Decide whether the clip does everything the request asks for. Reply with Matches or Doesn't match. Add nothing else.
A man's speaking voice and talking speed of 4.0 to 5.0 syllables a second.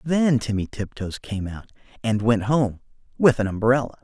Matches